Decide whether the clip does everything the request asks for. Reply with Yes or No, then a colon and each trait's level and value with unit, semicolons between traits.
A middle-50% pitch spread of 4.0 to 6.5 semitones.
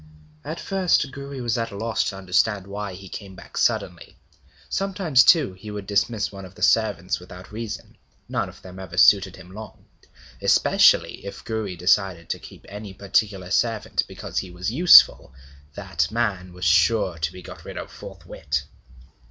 No: average, 3.5 semitones